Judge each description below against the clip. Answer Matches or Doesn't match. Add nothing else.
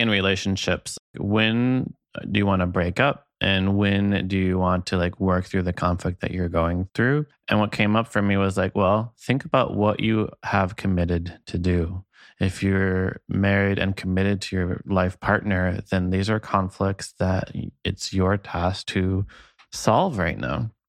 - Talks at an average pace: Matches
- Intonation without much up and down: Matches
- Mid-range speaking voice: Doesn't match